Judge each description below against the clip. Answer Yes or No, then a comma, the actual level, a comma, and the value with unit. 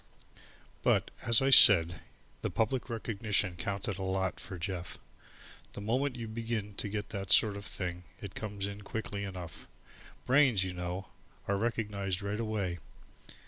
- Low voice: Yes, low, 100 Hz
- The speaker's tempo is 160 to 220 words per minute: No, average, 150 wpm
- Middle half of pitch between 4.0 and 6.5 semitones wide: No, average, 2.9 semitones